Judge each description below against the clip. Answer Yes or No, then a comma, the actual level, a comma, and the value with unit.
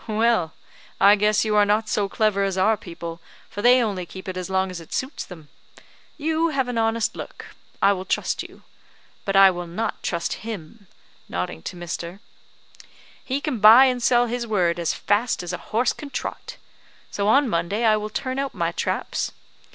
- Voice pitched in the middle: No, high, 210 Hz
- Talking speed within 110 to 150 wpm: No, average, 190 wpm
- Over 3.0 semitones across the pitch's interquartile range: Yes, average, 4.3 semitones